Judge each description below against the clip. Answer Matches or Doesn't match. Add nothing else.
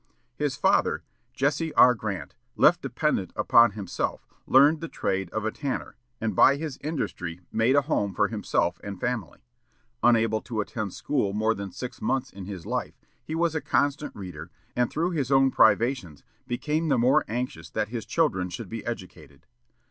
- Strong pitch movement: Matches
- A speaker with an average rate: Matches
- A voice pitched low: Matches